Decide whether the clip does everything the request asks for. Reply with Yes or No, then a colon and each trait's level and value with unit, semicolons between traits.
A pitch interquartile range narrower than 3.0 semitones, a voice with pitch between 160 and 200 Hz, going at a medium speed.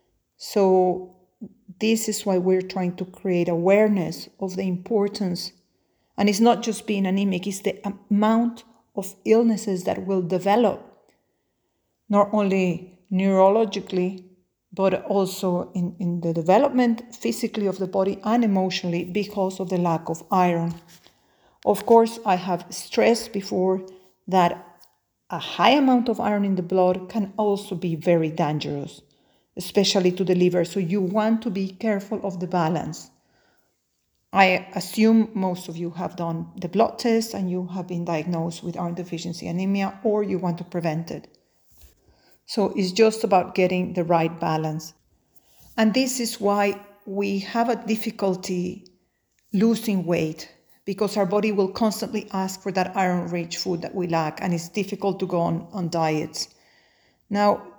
Yes: narrow, 2.5 semitones; high, 190 Hz; average, 150 wpm